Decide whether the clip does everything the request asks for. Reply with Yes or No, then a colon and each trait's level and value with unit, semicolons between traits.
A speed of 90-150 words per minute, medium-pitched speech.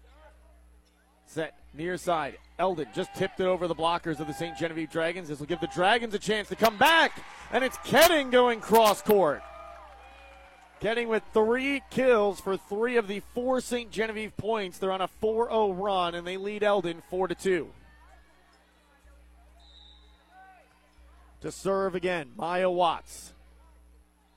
Yes: average, 140 wpm; medium, 180 Hz